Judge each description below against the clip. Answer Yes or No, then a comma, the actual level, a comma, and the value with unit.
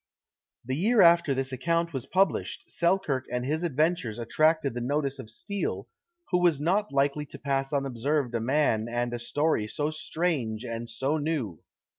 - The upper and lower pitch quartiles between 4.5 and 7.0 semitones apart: Yes, average, 5.2 semitones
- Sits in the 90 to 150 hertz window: Yes, medium, 140 Hz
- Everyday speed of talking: Yes, average, 165 wpm